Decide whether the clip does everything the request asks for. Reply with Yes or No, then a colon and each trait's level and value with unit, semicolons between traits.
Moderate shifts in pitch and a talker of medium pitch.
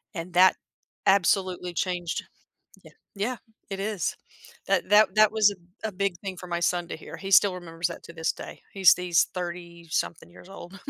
No: narrow, 2.3 semitones; medium, 180 Hz